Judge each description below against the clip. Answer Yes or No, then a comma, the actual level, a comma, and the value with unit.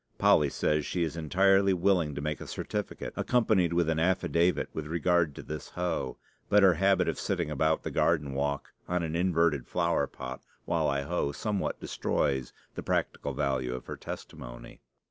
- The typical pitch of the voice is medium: No, very low, 80 Hz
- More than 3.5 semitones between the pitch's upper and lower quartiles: Yes, average, 3.9 semitones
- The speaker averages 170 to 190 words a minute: Yes, average, 175 wpm